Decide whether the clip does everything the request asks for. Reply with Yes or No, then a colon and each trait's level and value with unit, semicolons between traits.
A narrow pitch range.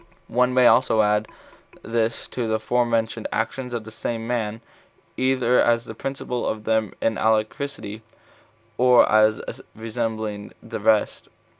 Yes: narrow, 2.1 semitones